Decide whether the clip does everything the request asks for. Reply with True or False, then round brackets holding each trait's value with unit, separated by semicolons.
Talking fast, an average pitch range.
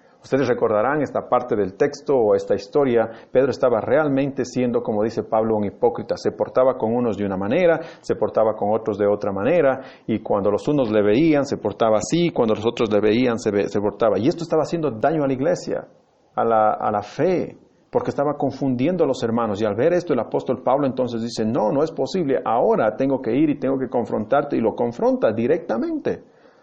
False (210 wpm; 5.8 semitones)